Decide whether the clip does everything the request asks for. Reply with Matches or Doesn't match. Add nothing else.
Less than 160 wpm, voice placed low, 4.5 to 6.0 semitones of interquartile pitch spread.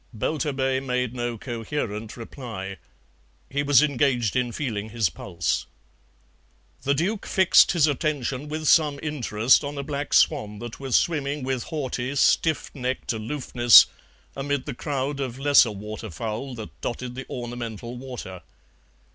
Doesn't match